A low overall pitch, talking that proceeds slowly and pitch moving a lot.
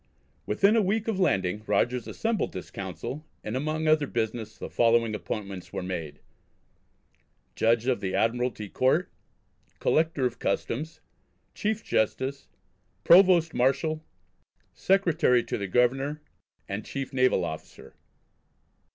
Yes: low, 125 Hz; slow, 120 wpm; wide, 6.5 semitones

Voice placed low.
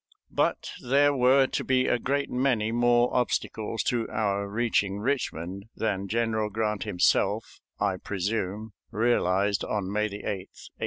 Yes: low, 110 Hz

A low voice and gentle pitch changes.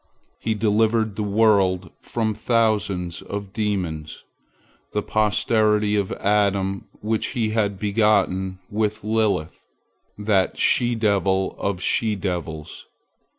Yes: low, 105 Hz; narrow, 2.2 semitones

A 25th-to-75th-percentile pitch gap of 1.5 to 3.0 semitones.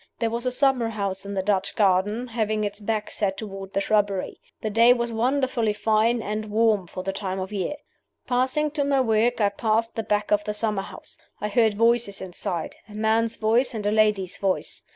Yes: narrow, 2.5 semitones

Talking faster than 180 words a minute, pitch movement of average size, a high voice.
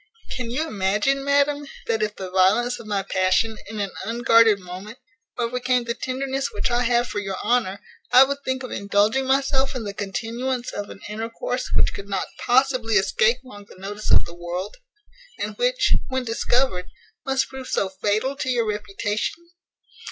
No: average, 175 wpm; average, 4.3 semitones; high, 230 Hz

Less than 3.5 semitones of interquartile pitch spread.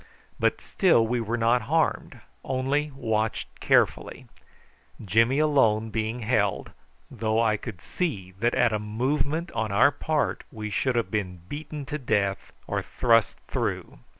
No: average, 4.5 semitones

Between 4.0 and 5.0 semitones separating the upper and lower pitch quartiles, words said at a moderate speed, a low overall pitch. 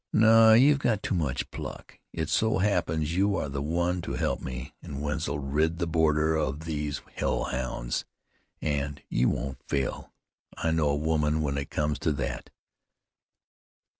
No: average, 3.2 semitones; average, 165 wpm; very low, 75 Hz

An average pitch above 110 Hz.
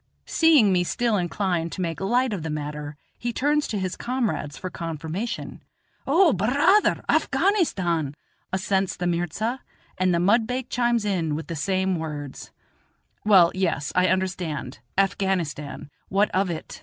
Yes: medium, 185 Hz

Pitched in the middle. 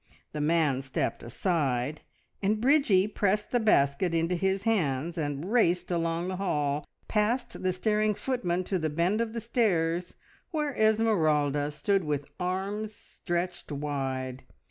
Yes: medium, 180 Hz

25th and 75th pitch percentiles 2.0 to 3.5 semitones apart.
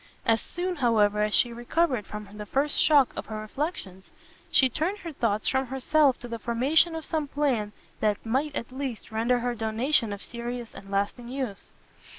No: average, 4.7 semitones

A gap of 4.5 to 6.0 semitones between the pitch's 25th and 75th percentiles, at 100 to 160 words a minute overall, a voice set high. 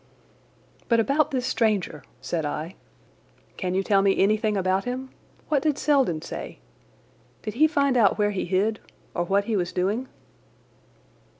Yes: wide, 5.4 semitones; average, 155 wpm; high, 210 Hz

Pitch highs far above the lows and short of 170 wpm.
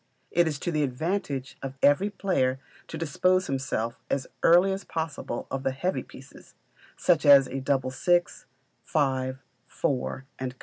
No: average, 4.7 semitones; average, 150 wpm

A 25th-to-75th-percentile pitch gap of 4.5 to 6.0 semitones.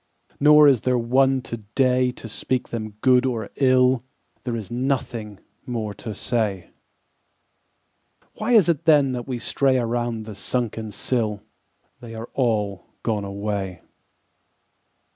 No: average, 3.3 semitones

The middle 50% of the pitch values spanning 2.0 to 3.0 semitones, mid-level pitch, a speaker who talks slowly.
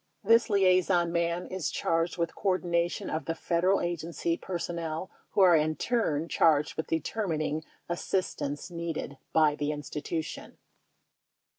Yes: narrow, 2.5 semitones; medium, 170 Hz; slow, 130 wpm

